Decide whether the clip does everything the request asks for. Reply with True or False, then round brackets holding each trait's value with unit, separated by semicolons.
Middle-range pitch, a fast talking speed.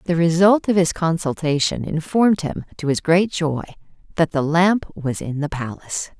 False (165 Hz; 175 wpm)